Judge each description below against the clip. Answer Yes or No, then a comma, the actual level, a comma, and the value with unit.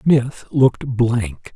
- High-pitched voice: No, low, 120 Hz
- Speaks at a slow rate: Yes, slow, 115 wpm